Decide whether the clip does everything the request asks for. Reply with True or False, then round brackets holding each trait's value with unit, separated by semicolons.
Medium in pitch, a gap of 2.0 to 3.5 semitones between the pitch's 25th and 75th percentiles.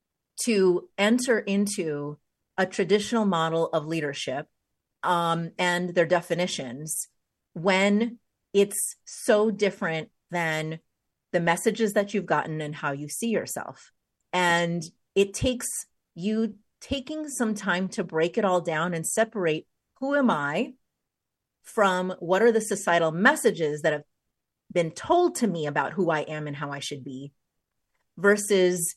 False (180 Hz; 4.6 semitones)